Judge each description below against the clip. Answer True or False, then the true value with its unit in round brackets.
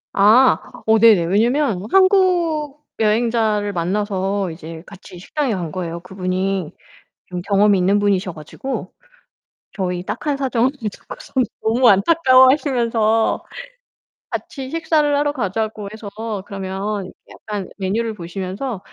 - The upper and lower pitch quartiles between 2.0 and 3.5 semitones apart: False (5.4 semitones)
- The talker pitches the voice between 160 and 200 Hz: False (210 Hz)